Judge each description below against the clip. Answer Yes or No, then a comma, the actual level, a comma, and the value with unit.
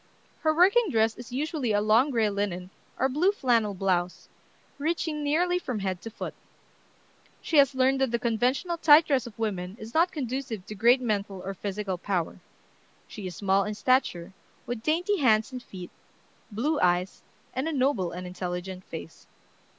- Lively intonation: Yes, wide, 6.4 semitones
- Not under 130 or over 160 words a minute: No, average, 170 wpm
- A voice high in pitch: Yes, high, 230 Hz